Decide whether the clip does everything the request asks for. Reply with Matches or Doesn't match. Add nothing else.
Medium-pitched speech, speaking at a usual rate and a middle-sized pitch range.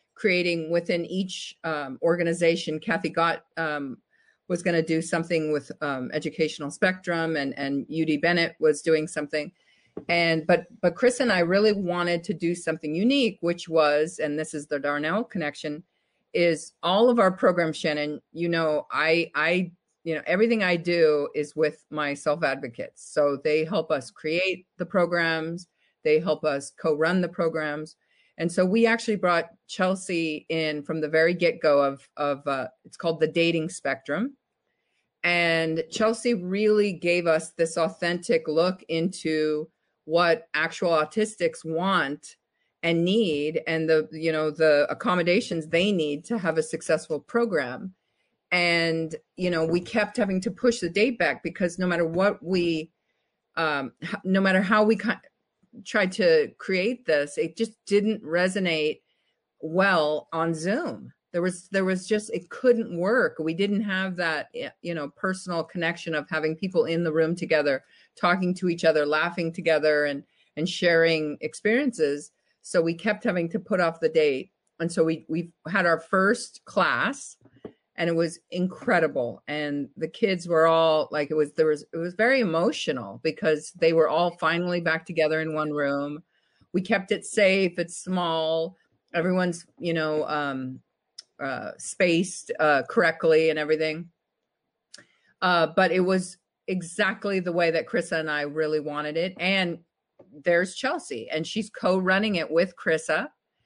Matches